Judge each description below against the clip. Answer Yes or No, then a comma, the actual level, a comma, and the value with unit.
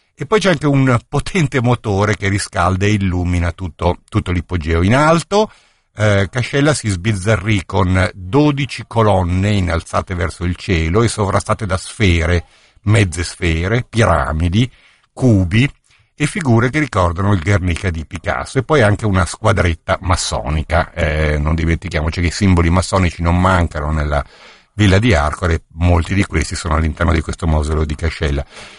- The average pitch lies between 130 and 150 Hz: No, very low, 95 Hz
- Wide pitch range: No, average, 4.5 semitones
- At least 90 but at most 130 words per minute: No, average, 150 wpm